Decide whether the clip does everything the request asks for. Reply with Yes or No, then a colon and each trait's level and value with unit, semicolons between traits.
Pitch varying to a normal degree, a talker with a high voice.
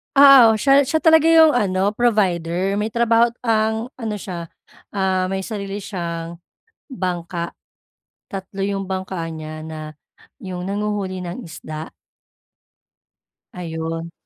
Yes: average, 4.5 semitones; high, 195 Hz